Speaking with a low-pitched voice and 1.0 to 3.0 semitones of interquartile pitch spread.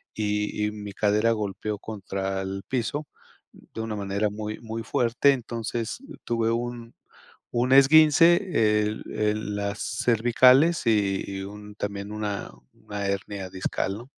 Yes: low, 110 Hz; average, 2.7 semitones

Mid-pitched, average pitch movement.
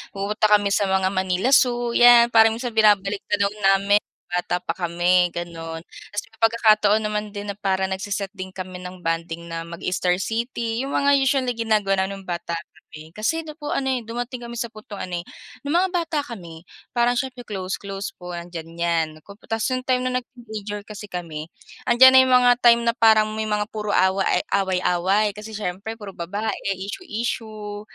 No: high, 205 Hz; average, 4.0 semitones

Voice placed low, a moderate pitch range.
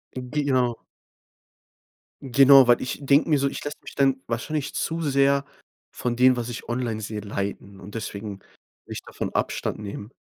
Yes: low, 125 Hz; average, 4.1 semitones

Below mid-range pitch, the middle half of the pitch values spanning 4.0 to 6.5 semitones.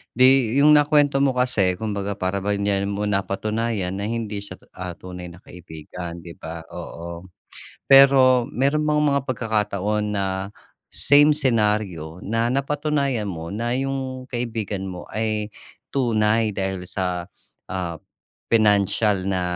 Yes: low, 105 Hz; wide, 5.4 semitones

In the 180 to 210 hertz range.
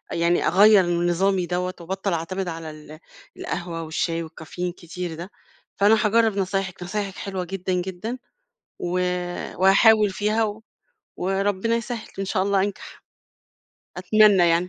Yes: high, 190 Hz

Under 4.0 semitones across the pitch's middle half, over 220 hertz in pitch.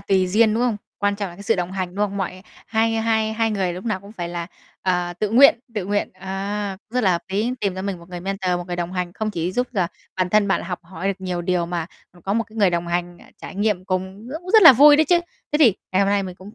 No: average, 3.3 semitones; high, 195 Hz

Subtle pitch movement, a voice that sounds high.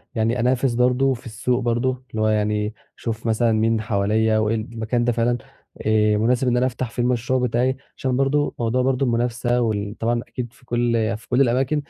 No: narrow, 2.2 semitones; low, 120 Hz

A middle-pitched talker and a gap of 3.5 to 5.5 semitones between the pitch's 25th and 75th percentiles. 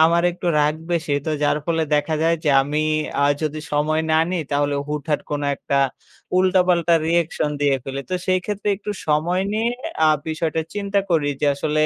No: medium, 160 Hz; average, 2.8 semitones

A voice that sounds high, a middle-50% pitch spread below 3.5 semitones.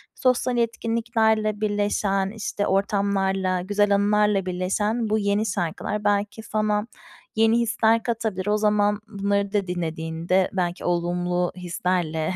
Yes: high, 205 Hz; average, 2.7 semitones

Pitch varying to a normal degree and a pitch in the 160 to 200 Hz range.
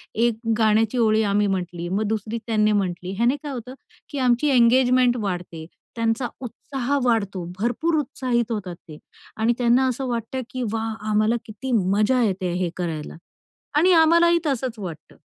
No: average, 3.9 semitones; high, 225 Hz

